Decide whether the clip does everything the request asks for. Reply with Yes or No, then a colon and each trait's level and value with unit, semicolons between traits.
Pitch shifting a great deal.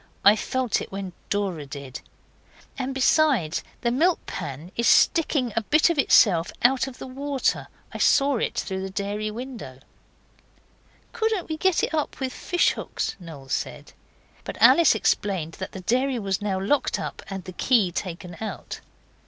Yes: wide, 6.4 semitones